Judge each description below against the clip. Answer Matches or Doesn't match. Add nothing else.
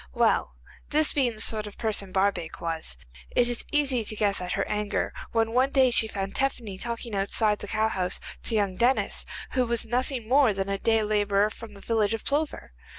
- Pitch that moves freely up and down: Doesn't match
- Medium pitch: Doesn't match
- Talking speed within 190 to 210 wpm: Matches